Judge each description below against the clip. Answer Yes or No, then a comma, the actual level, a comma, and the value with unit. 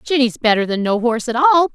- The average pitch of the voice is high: Yes, very high, 250 Hz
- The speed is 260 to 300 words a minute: No, fast, 240 wpm